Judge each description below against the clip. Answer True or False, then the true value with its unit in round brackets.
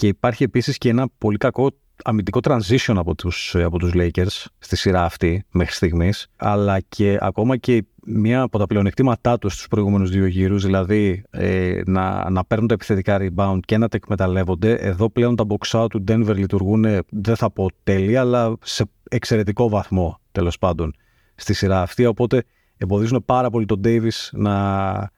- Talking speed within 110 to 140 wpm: False (170 wpm)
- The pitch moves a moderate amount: True (3.3 semitones)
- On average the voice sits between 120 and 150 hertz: False (105 Hz)